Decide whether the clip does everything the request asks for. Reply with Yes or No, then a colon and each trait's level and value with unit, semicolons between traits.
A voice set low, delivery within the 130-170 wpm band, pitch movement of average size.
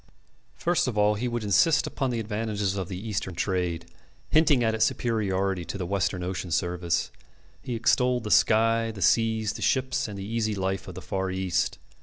No: low, 105 Hz; average, 190 wpm; average, 3.4 semitones